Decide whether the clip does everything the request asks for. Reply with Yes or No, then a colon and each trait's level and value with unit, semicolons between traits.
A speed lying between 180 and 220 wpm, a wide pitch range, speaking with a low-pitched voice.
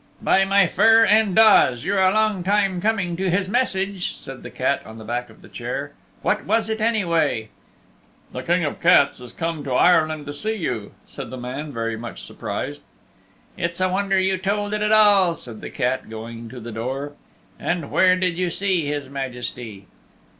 No: average, 195 wpm; wide, 7.5 semitones; medium, 175 Hz